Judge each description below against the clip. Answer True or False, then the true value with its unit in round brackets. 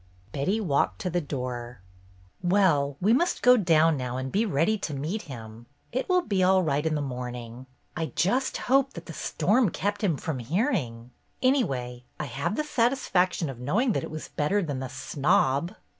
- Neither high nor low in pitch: True (160 Hz)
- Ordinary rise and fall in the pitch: False (7.7 semitones)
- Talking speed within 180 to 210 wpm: True (190 wpm)